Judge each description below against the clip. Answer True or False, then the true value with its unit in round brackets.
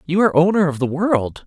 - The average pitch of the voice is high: False (170 Hz)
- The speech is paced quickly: True (245 wpm)